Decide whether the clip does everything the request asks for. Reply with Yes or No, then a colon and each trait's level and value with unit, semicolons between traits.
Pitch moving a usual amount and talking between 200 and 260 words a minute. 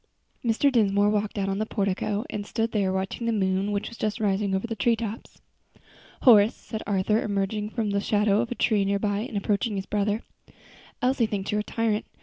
No: narrow, 1.9 semitones; fast, 205 wpm